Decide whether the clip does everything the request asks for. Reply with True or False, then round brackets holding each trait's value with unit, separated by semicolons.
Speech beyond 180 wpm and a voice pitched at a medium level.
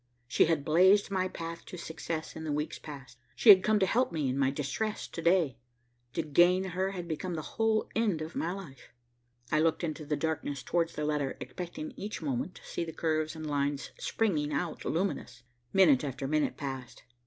True (200 wpm; 160 Hz)